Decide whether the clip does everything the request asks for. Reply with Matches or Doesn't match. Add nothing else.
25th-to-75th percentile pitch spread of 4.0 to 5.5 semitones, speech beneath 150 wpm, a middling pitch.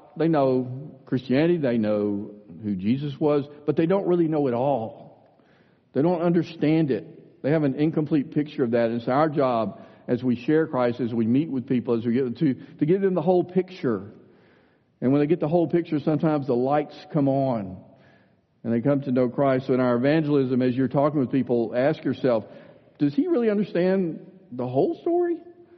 Doesn't match